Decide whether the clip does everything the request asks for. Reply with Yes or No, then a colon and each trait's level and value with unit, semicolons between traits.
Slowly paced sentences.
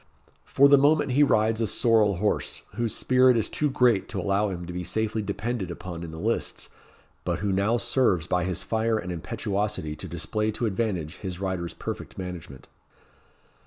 No: average, 180 wpm